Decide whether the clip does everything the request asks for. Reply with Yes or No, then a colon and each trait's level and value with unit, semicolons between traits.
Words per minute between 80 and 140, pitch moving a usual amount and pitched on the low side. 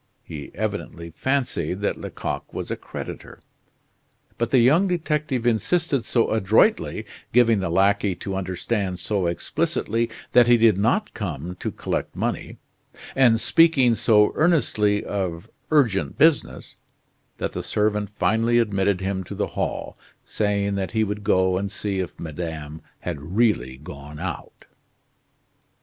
Yes: slow, 135 wpm; average, 4.3 semitones; low, 105 Hz